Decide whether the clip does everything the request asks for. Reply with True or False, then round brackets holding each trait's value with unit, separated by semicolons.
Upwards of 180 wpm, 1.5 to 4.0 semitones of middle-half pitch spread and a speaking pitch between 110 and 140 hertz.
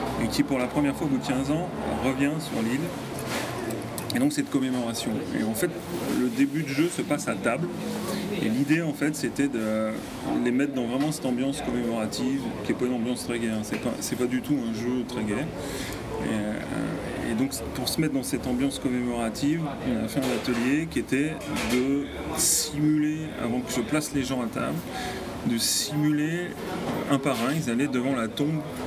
True (200 wpm; 3.4 semitones; 135 Hz)